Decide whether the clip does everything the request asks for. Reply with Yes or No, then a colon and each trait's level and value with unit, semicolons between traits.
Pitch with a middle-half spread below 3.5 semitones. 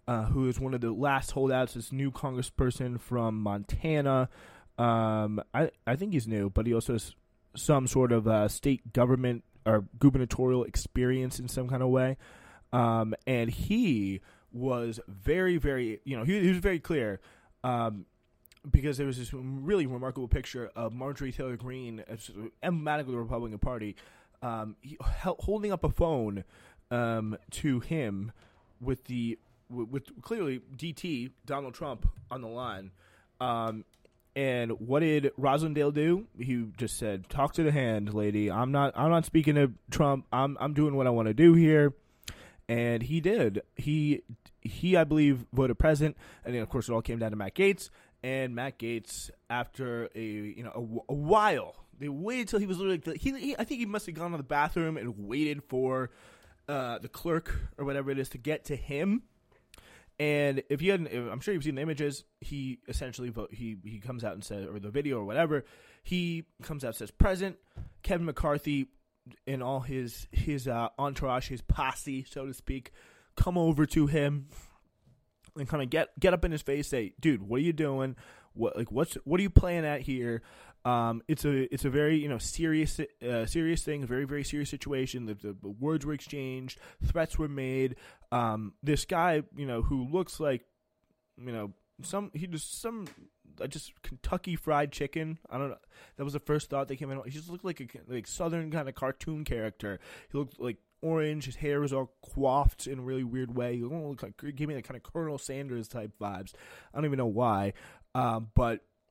No: average, 4.3 semitones